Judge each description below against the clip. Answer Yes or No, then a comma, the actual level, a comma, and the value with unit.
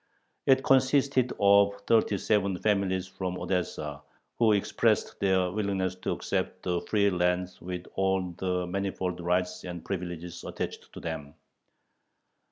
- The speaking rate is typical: No, slow, 130 wpm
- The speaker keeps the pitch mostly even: Yes, narrow, 2.1 semitones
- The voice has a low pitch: Yes, very low, 95 Hz